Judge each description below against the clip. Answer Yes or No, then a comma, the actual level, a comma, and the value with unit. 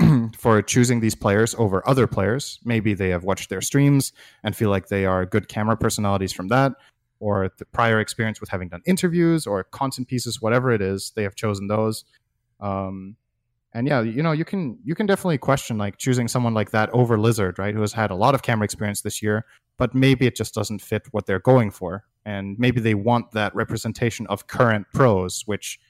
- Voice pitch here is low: Yes, low, 110 Hz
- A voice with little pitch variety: No, average, 3.4 semitones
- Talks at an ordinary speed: No, fast, 210 wpm